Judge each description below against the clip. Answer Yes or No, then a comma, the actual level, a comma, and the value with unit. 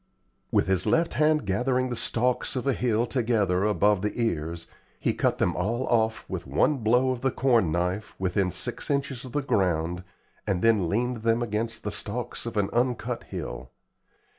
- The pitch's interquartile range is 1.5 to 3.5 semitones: No, average, 4.3 semitones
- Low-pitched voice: Yes, low, 115 Hz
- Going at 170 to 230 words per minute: Yes, average, 180 wpm